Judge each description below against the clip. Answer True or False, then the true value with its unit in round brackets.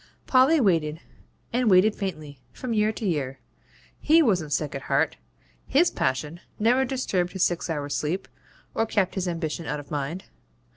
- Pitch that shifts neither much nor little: False (6.7 semitones)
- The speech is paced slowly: False (160 wpm)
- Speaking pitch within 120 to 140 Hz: False (180 Hz)